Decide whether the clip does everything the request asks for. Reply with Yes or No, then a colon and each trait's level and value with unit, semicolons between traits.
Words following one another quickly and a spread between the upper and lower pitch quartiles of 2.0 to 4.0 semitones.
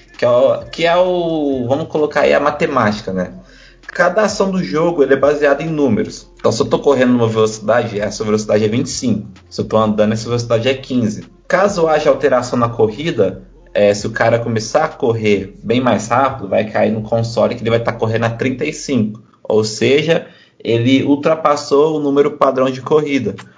No: fast, 195 wpm; average, 5.3 semitones